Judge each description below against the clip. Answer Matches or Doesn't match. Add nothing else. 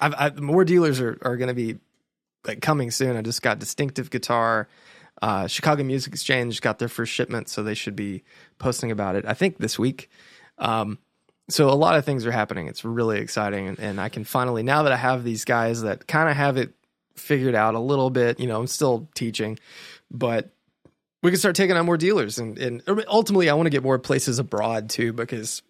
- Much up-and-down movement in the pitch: Doesn't match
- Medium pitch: Doesn't match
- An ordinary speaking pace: Doesn't match